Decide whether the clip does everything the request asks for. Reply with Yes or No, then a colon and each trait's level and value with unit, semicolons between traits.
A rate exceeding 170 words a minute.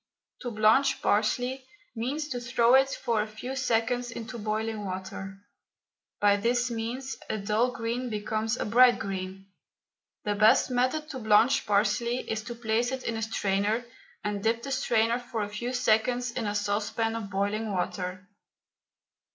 No: average, 160 wpm